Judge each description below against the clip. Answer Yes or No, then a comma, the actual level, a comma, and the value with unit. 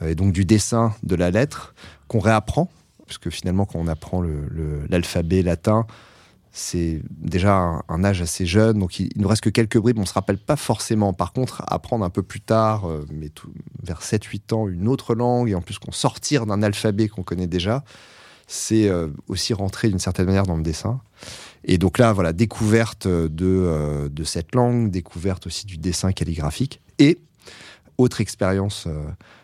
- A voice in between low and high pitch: No, low, 100 Hz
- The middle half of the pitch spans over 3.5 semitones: Yes, average, 4.2 semitones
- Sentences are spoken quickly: No, average, 185 wpm